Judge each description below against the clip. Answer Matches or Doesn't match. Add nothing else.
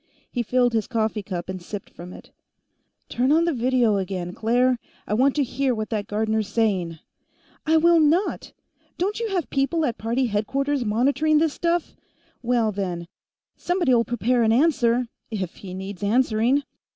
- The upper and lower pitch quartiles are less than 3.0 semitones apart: Doesn't match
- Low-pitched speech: Doesn't match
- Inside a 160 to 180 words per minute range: Matches